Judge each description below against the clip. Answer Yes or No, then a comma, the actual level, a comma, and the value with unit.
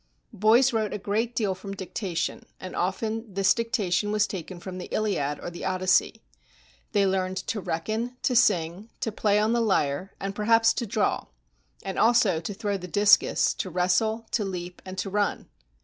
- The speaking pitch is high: Yes, high, 200 Hz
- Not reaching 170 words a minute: No, average, 180 wpm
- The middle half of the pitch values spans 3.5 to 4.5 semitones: No, average, 3.0 semitones